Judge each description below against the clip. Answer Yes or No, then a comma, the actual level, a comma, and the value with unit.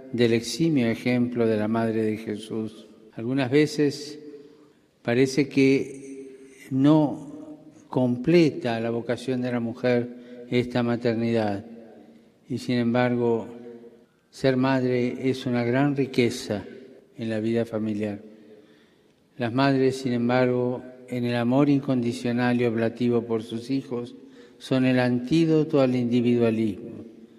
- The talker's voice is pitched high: No, low, 120 Hz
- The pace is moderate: No, slow, 115 wpm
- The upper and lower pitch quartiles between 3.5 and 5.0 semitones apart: No, narrow, 2.4 semitones